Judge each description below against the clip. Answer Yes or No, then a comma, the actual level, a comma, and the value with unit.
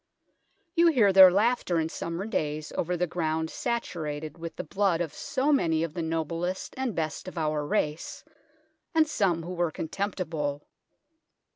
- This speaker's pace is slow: No, average, 155 wpm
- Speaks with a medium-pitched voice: Yes, medium, 170 Hz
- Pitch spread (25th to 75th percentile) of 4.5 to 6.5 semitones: No, average, 3.7 semitones